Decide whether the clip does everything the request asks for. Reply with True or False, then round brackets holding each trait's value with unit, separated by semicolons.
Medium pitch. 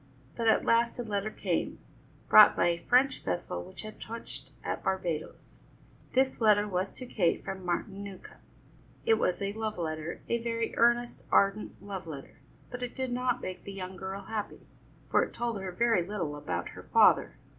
False (200 Hz)